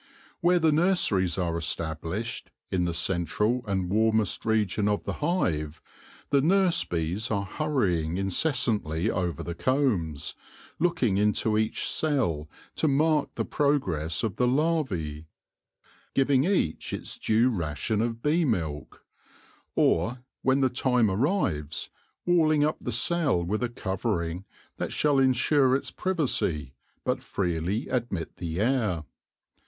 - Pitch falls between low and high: No, low, 110 Hz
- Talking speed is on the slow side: Yes, slow, 130 wpm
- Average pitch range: No, wide, 8.2 semitones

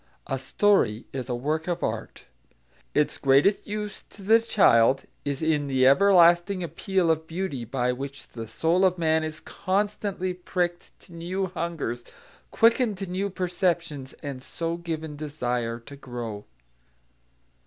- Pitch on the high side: No, medium, 165 Hz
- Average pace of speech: Yes, average, 145 wpm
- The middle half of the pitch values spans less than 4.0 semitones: No, wide, 5.6 semitones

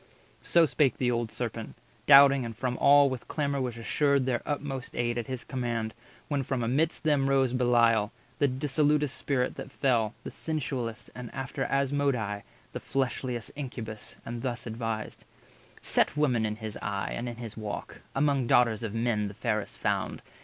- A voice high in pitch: No, low, 125 Hz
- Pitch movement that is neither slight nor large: Yes, average, 3.2 semitones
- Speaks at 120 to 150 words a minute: No, average, 170 wpm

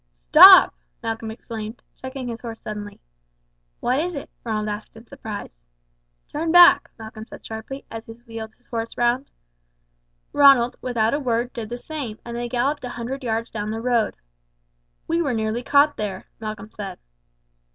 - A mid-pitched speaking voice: No, high, 230 Hz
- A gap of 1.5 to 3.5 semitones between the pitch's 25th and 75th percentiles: Yes, average, 2.7 semitones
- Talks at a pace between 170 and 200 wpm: No, average, 160 wpm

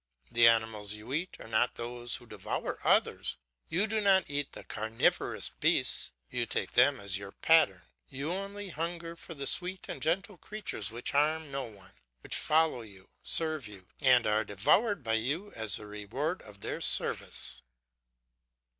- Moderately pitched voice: No, low, 130 Hz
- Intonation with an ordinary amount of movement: No, wide, 7.3 semitones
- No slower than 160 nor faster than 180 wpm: Yes, average, 165 wpm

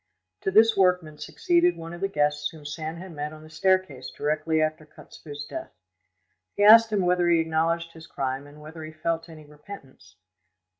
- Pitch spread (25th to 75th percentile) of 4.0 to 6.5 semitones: No, average, 3.2 semitones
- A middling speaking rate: Yes, average, 185 wpm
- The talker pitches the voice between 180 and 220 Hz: No, medium, 160 Hz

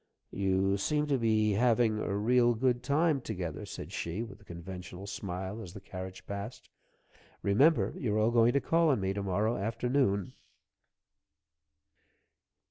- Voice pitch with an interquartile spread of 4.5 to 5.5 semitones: No, average, 4.0 semitones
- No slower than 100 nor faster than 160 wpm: Yes, average, 150 wpm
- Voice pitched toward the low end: Yes, low, 105 Hz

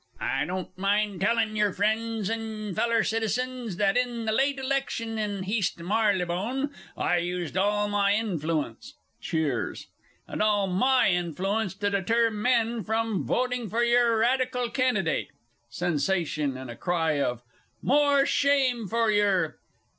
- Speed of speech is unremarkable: No, slow, 130 wpm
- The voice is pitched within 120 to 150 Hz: No, high, 210 Hz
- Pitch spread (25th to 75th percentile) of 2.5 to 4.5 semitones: Yes, average, 4.2 semitones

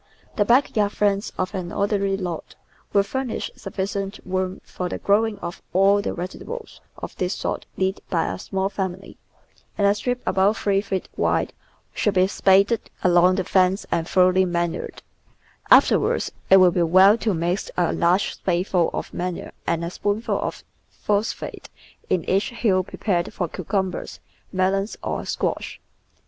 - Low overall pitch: No, high, 190 Hz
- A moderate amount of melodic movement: No, narrow, 1.9 semitones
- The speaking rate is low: No, average, 170 wpm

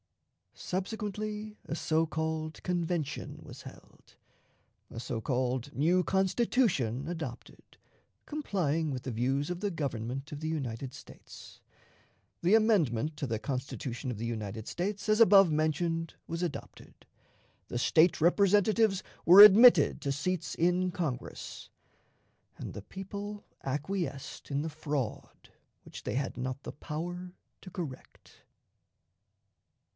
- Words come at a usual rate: No, slow, 125 wpm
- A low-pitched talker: No, medium, 160 Hz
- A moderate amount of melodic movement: No, wide, 5.7 semitones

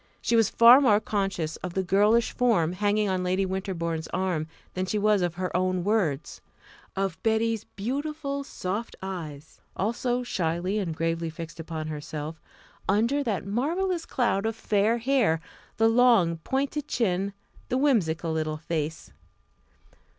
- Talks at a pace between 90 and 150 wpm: Yes, average, 145 wpm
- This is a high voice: Yes, high, 195 Hz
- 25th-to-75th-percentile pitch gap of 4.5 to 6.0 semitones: Yes, wide, 5.4 semitones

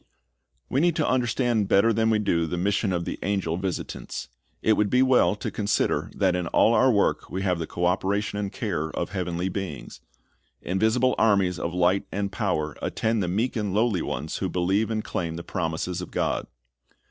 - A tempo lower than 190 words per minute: No, average, 195 wpm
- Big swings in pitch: No, average, 3.7 semitones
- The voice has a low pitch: Yes, low, 100 Hz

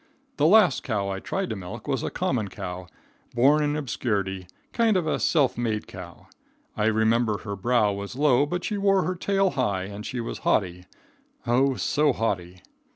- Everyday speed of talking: Yes, average, 180 wpm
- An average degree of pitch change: No, wide, 6.9 semitones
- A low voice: Yes, low, 120 Hz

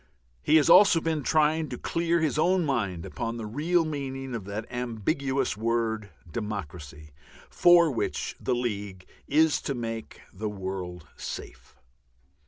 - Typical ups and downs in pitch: No, wide, 6.9 semitones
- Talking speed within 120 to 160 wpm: Yes, average, 140 wpm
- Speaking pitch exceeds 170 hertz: No, low, 120 Hz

